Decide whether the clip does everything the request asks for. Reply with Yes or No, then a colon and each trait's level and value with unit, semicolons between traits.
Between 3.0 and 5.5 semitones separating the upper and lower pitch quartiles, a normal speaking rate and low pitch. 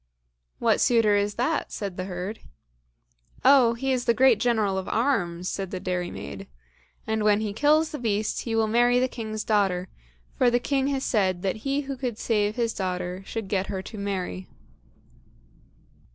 No: average, 4.2 semitones; average, 175 wpm; high, 215 Hz